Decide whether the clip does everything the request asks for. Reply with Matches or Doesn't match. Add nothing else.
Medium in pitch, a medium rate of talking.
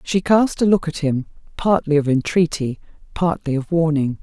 Matches